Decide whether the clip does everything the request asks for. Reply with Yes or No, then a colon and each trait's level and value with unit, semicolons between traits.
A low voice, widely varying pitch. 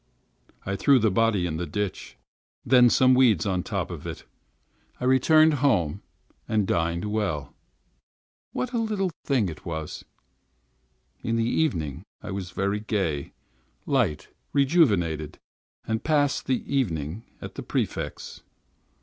Yes: low, 105 Hz; wide, 7.2 semitones